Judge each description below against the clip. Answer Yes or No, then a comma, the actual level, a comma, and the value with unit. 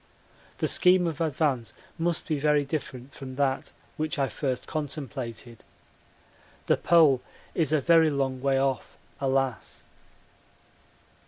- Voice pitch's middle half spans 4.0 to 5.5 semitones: No, average, 2.9 semitones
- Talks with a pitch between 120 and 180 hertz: Yes, medium, 140 Hz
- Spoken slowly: Yes, slow, 120 wpm